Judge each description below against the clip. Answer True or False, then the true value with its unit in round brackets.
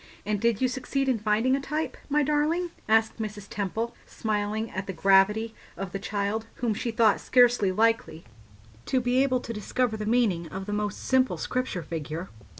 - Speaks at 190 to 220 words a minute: False (180 wpm)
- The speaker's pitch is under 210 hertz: False (220 Hz)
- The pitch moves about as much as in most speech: True (3.9 semitones)